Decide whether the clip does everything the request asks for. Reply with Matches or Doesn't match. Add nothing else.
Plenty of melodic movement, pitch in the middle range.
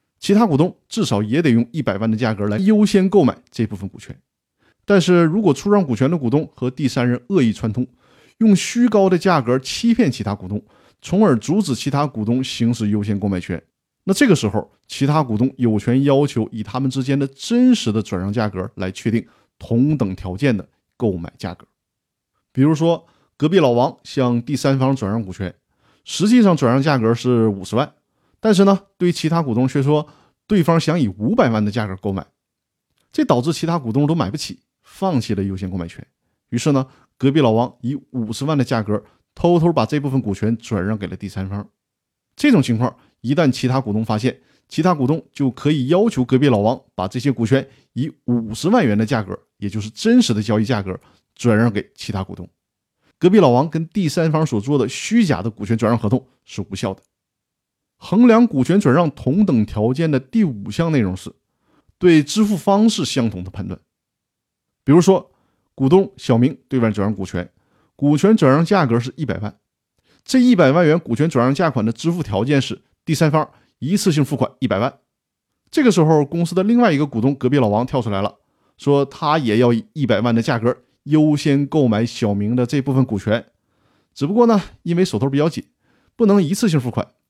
Doesn't match